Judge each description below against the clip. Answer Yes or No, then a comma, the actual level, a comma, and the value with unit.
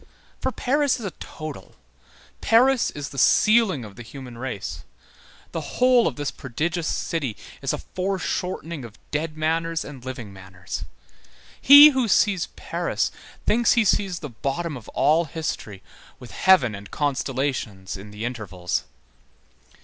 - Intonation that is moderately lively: No, wide, 8.0 semitones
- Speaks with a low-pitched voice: No, medium, 150 Hz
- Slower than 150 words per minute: Yes, average, 140 wpm